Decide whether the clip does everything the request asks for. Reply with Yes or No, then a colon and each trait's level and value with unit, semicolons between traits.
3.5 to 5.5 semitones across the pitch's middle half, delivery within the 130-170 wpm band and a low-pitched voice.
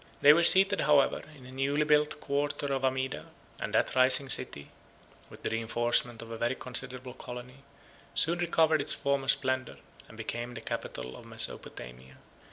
No: average, 2.8 semitones; average, 165 wpm; low, 130 Hz